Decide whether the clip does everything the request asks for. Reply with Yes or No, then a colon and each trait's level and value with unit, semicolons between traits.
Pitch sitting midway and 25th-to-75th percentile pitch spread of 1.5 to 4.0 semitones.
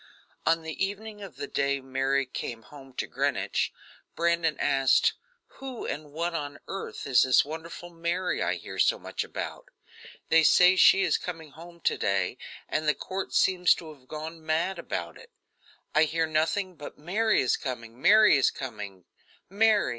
No: medium, 160 Hz; average, 4.6 semitones